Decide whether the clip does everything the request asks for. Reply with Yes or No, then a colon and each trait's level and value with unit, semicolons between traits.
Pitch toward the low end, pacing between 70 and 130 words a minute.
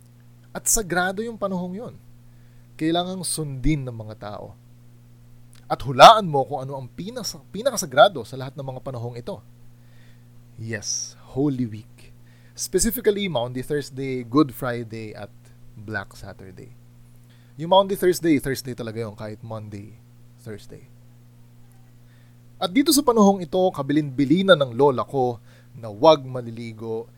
Yes: low, 120 Hz; average, 125 wpm